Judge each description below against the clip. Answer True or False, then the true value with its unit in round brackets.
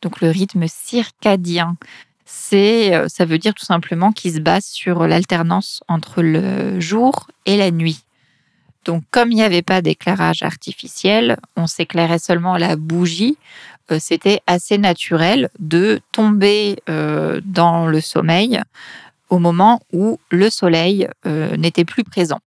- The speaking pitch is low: False (175 Hz)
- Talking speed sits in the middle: False (135 wpm)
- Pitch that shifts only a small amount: False (3.5 semitones)